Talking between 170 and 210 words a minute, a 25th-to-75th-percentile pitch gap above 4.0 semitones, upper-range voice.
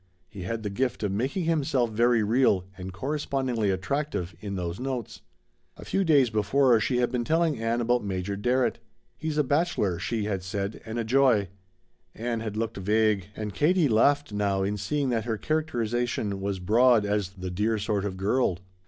No: average, 180 wpm; average, 4.5 semitones; low, 110 Hz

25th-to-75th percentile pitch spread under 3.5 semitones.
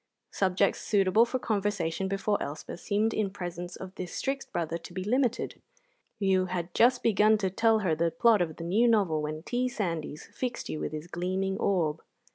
No: average, 4.0 semitones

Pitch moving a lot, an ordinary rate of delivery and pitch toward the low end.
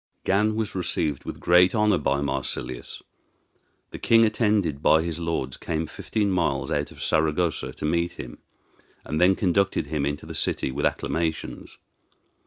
No: average, 4.8 semitones; average, 155 wpm; very low, 85 Hz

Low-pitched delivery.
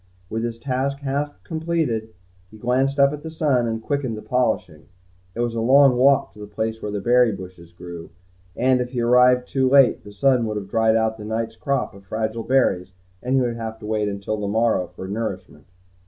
Yes: low, 115 Hz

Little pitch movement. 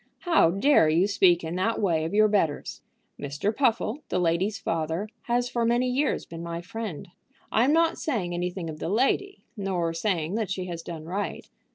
No: wide, 5.4 semitones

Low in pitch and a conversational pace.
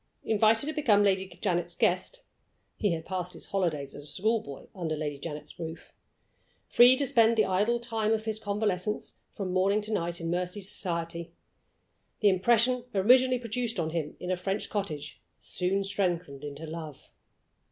No: high, 190 Hz; average, 165 wpm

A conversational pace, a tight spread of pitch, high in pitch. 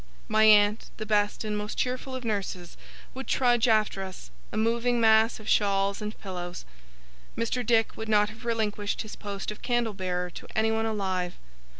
Yes: average, 175 wpm; narrow, 2.1 semitones; high, 215 Hz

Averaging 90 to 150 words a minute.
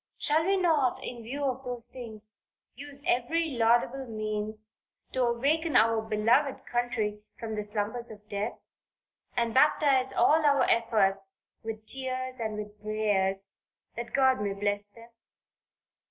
Yes: average, 140 wpm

